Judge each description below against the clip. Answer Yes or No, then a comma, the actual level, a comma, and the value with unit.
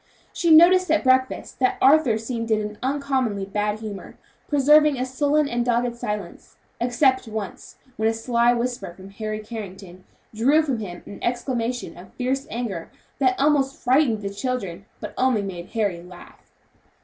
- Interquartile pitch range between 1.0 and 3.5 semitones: No, average, 4.1 semitones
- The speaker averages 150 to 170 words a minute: Yes, average, 160 wpm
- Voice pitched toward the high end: Yes, high, 240 Hz